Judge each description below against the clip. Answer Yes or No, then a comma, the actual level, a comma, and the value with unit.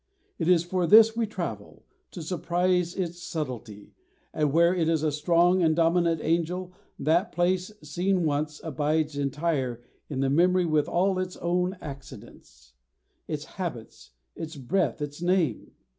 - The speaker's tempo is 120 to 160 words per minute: Yes, average, 145 wpm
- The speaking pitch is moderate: Yes, medium, 170 Hz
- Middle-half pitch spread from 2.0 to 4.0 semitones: Yes, average, 3.2 semitones